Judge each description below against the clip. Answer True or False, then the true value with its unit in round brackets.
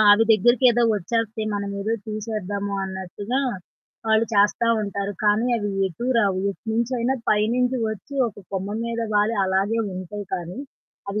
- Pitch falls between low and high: False (210 Hz)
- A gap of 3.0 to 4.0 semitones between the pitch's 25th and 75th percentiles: False (2.4 semitones)